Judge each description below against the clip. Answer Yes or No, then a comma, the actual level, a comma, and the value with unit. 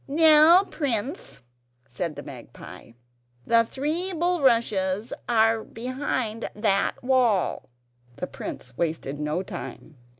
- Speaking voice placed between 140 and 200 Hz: No, high, 230 Hz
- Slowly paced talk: Yes, slow, 100 wpm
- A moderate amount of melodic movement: No, wide, 7.2 semitones